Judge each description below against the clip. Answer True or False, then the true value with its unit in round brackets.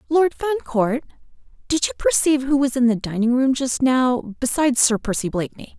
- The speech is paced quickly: False (175 wpm)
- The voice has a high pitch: True (255 Hz)